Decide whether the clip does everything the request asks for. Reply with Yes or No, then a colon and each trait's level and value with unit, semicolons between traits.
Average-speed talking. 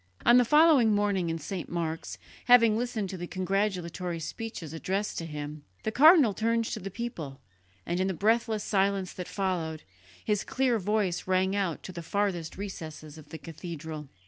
Yes: average, 170 wpm